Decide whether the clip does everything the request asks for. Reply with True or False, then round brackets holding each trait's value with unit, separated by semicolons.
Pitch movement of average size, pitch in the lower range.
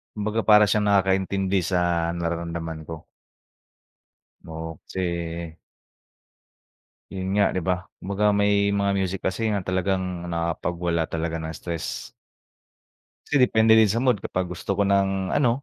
True (3.1 semitones; 95 Hz)